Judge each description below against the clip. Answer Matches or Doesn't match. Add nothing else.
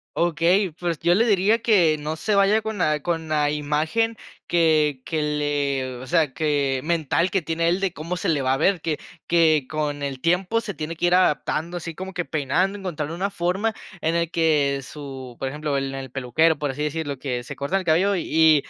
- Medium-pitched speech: Matches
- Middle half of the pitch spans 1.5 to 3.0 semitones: Doesn't match